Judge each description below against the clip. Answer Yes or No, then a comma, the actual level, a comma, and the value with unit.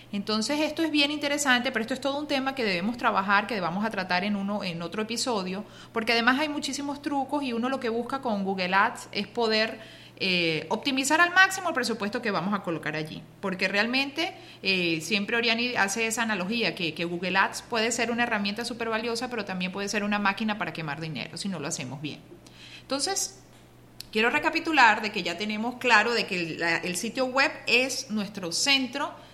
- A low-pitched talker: No, high, 225 Hz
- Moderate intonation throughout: Yes, average, 5.0 semitones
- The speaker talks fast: Yes, fast, 205 wpm